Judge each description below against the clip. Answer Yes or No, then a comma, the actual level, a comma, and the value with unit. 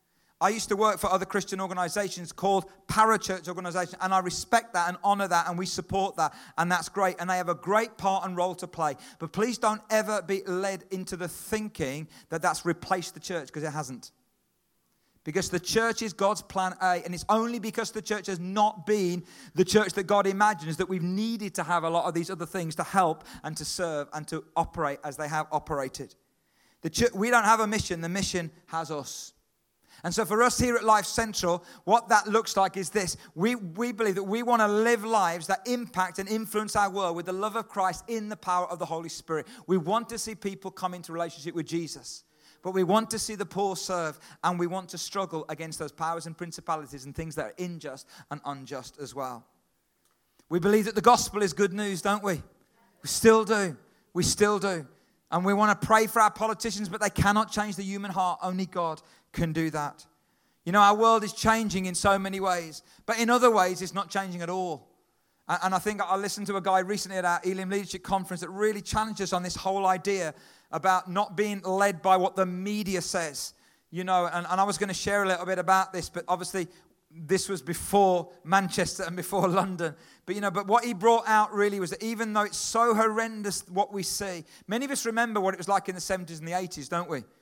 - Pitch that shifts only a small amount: No, average, 3.1 semitones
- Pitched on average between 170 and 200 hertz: Yes, high, 190 Hz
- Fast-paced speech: Yes, fast, 225 wpm